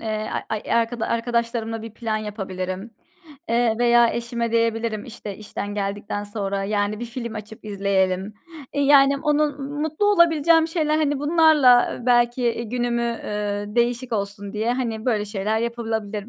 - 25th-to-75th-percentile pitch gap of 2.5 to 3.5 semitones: Yes, average, 2.8 semitones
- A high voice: Yes, high, 230 Hz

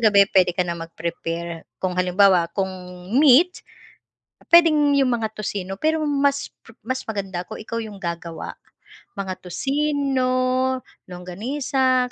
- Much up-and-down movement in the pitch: Yes, wide, 7.0 semitones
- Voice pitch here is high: Yes, high, 215 Hz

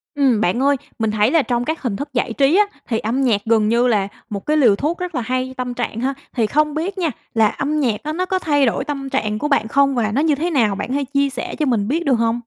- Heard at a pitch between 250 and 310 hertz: Yes, very high, 260 Hz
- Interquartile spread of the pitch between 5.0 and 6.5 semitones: No, average, 4.6 semitones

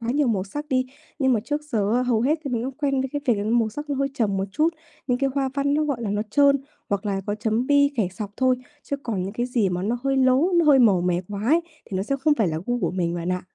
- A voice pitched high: Yes, high, 245 Hz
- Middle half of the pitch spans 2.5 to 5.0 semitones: No, wide, 5.4 semitones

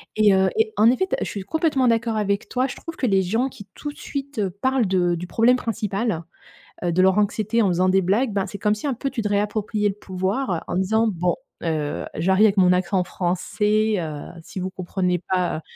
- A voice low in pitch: No, high, 205 Hz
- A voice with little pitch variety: No, average, 3.7 semitones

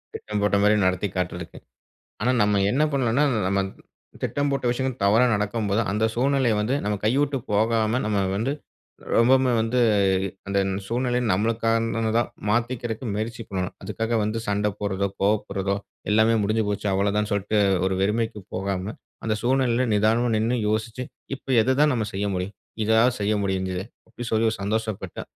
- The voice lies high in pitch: No, low, 110 Hz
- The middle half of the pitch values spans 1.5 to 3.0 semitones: Yes, average, 2.7 semitones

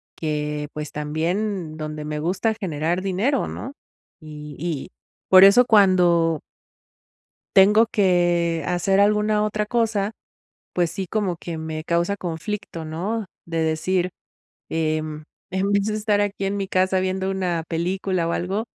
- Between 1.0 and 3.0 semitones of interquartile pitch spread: No, average, 3.9 semitones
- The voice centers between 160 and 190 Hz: Yes, medium, 185 Hz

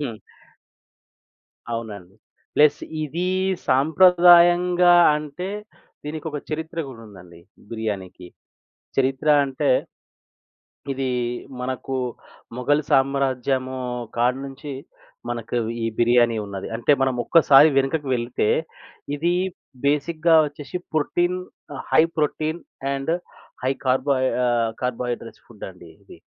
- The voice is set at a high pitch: No, low, 135 Hz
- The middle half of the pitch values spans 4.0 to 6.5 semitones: Yes, average, 4.5 semitones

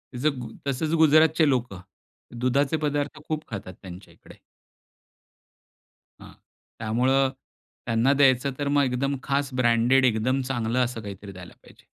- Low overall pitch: Yes, low, 130 Hz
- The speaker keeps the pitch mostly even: No, average, 3.7 semitones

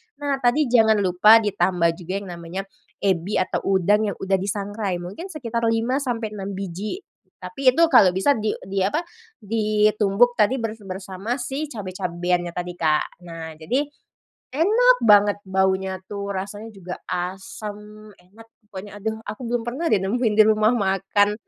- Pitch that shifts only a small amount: No, average, 3.2 semitones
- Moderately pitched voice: No, high, 205 Hz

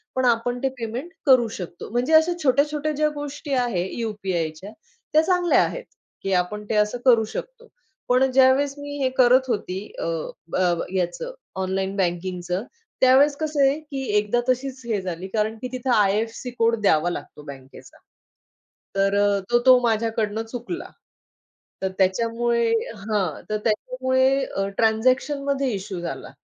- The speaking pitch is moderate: No, high, 230 Hz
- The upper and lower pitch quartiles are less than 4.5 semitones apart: No, average, 5.3 semitones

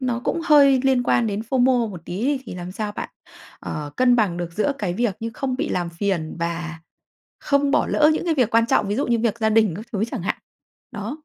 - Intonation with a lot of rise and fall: Yes, wide, 5.7 semitones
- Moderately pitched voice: No, high, 225 Hz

